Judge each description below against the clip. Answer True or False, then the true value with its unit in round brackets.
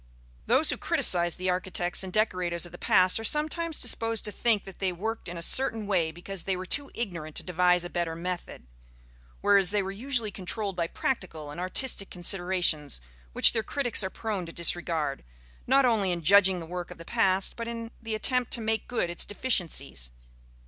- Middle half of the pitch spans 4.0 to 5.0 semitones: True (4.3 semitones)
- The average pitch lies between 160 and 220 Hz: True (190 Hz)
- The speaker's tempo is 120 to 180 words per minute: False (195 wpm)